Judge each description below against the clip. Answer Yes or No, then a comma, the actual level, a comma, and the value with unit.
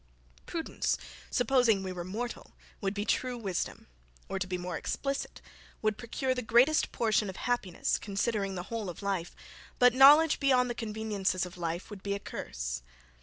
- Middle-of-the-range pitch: No, high, 215 Hz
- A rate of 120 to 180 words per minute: Yes, average, 170 wpm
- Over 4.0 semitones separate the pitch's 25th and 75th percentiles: Yes, average, 4.6 semitones